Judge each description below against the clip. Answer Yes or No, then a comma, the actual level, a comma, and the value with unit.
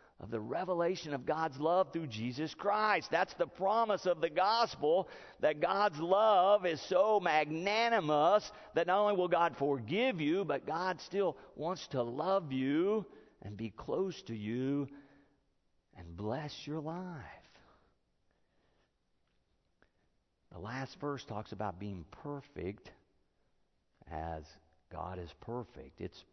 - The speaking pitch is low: No, medium, 145 Hz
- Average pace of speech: No, slow, 130 wpm